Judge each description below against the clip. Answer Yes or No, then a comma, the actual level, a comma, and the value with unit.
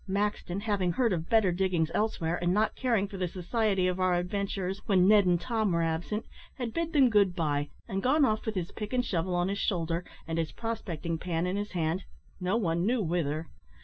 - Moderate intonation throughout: Yes, average, 3.7 semitones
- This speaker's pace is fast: Yes, fast, 210 wpm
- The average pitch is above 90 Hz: Yes, high, 190 Hz